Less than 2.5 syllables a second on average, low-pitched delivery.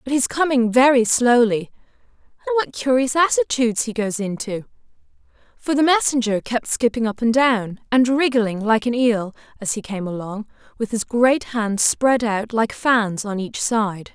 No: 2.0 syllables/s; high, 235 Hz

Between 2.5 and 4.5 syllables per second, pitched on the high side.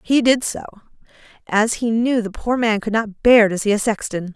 No: 5.0 syllables/s; high, 220 Hz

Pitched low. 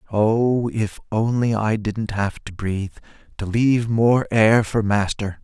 Yes: low, 110 Hz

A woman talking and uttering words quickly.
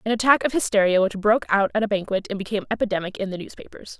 Yes: female; fast, 240 wpm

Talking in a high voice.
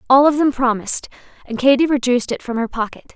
Yes: very high, 250 Hz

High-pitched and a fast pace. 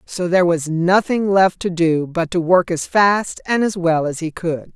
No: medium, 180 Hz; fast, 225 wpm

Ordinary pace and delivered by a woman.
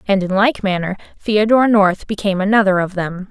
Yes: average, 180 wpm; female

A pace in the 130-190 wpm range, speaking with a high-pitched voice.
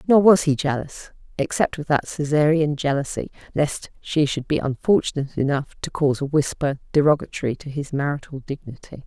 No: average, 160 wpm; medium, 145 Hz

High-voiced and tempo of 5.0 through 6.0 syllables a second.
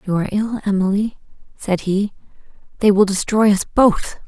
Yes: high, 200 Hz; 5.1 syllables/s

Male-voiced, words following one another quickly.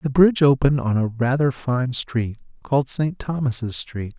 No: male; average, 170 wpm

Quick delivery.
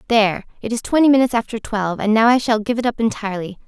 Yes: fast, 245 wpm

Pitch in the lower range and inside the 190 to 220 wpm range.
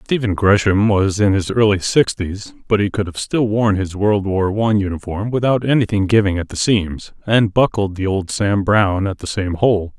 Yes: low, 100 Hz; fast, 205 wpm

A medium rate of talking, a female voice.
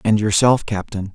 No: average, 160 wpm; male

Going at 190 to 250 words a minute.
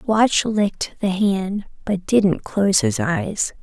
No: average, 150 wpm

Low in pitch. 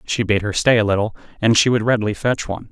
Yes: low, 110 Hz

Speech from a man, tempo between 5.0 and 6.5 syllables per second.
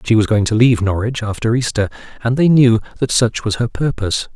Yes: male; 6.0 syllables/s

